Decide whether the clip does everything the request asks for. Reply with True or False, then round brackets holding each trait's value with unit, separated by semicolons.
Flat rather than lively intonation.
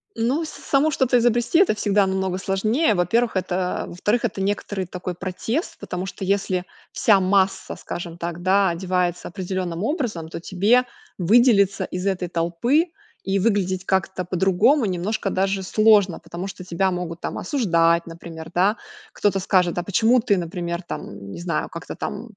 False (3.2 semitones)